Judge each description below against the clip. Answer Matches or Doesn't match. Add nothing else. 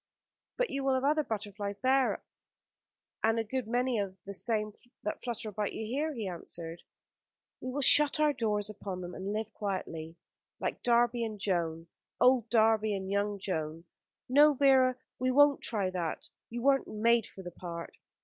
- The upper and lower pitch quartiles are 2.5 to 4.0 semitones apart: Doesn't match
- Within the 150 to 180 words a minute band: Matches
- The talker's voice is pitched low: Doesn't match